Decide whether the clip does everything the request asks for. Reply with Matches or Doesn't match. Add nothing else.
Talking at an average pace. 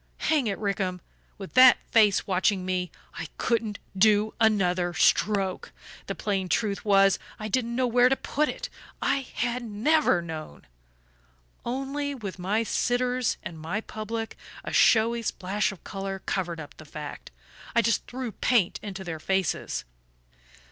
Matches